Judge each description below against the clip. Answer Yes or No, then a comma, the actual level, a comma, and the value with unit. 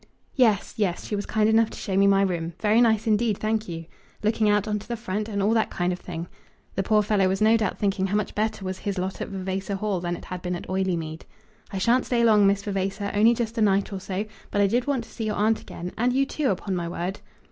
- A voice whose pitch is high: Yes, high, 205 Hz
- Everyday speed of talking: No, fast, 260 wpm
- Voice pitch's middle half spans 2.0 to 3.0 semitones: Yes, narrow, 2.6 semitones